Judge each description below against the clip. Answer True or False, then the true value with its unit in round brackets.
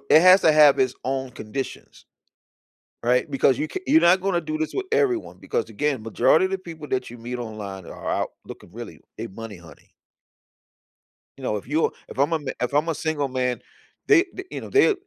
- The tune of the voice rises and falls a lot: True (6.4 semitones)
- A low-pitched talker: False (150 Hz)